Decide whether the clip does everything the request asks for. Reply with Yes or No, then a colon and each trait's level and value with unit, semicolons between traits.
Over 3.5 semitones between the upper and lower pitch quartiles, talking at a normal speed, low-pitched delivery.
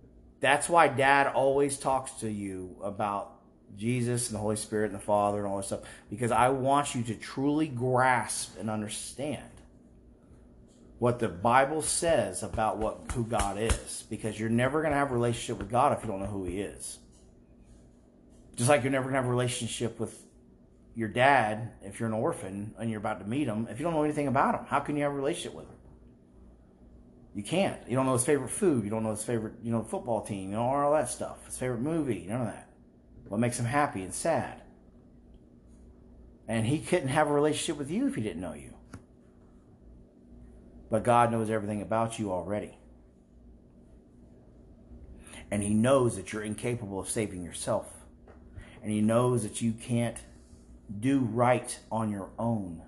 Yes: wide, 5.4 semitones; average, 190 wpm; low, 110 Hz